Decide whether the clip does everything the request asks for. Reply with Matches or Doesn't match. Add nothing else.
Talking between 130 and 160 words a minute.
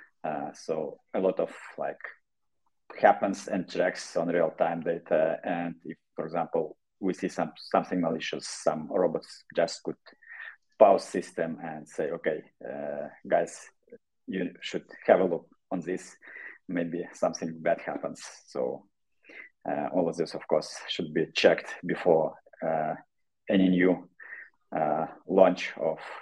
Matches